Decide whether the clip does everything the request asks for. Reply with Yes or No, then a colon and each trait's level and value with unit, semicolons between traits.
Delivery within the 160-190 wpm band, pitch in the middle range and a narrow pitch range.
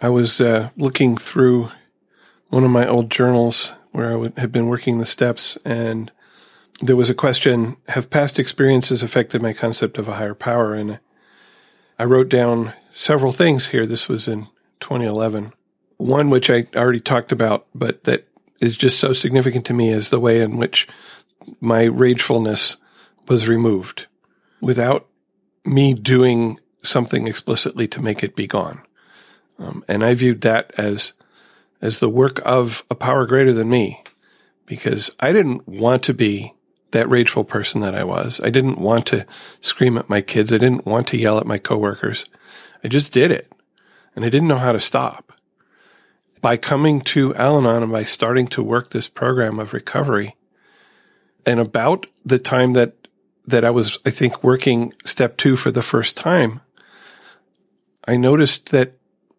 No: average, 165 wpm; low, 120 Hz; narrow, 2.1 semitones